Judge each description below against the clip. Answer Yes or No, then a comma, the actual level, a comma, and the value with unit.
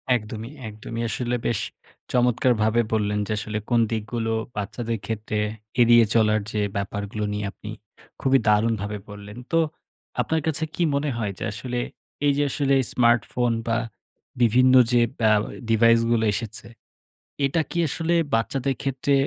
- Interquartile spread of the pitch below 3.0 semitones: Yes, narrow, 2.6 semitones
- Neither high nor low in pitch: No, low, 115 Hz